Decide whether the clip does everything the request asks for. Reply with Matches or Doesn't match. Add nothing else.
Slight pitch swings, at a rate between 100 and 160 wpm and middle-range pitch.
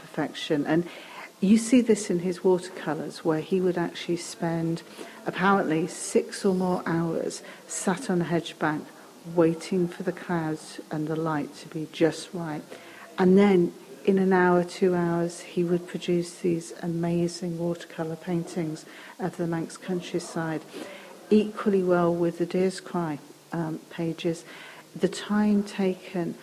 Matches